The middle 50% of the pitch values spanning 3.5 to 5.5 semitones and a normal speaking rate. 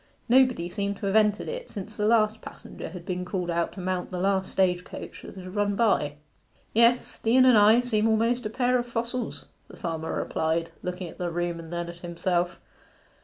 No: average, 4.5 semitones; fast, 210 wpm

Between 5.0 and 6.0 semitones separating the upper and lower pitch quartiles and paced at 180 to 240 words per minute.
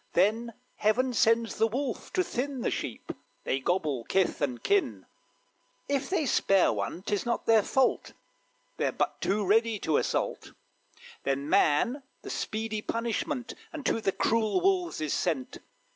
No: wide, 5.5 semitones; average, 145 wpm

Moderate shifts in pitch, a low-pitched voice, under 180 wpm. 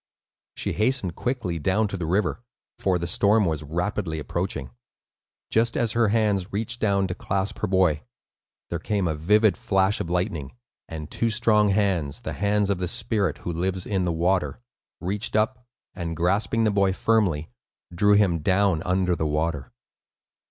Yes: average, 3.7 semitones; very low, 95 Hz; average, 165 wpm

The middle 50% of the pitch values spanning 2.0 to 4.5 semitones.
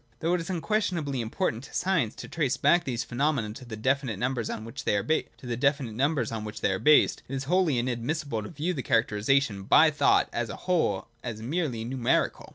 No: average, 5.2 semitones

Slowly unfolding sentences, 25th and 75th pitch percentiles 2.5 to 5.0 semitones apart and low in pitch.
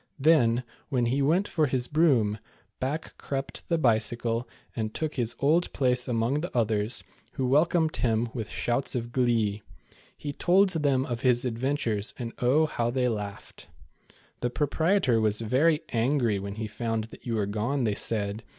No: average, 170 wpm; average, 4.2 semitones; low, 125 Hz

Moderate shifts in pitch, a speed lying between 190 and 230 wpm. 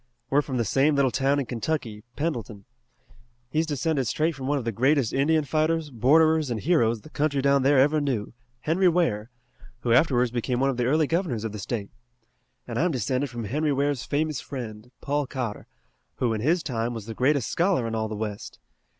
Yes: average, 4.6 semitones; average, 200 wpm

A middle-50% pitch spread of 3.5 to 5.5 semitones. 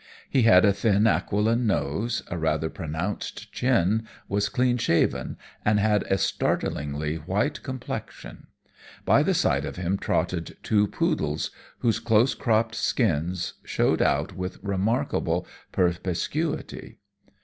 Yes: average, 4.4 semitones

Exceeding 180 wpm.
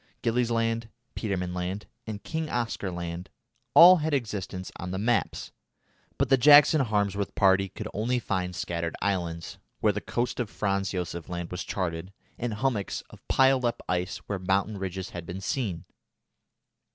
No: average, 160 wpm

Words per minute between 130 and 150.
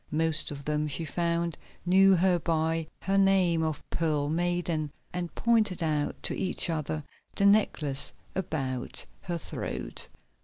Yes: average, 140 wpm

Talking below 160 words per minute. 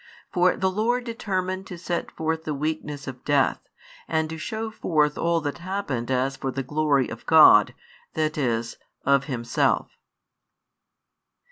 Yes: average, 145 wpm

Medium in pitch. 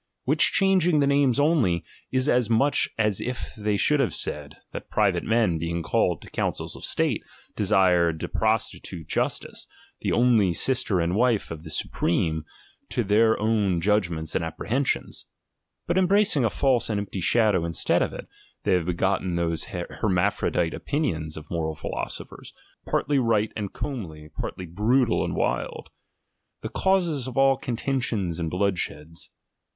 No: low, 105 Hz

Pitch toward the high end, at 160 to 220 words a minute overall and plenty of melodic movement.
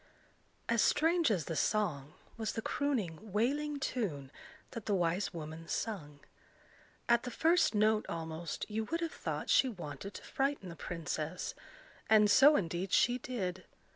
No: high, 210 Hz; average, 150 wpm; wide, 6.8 semitones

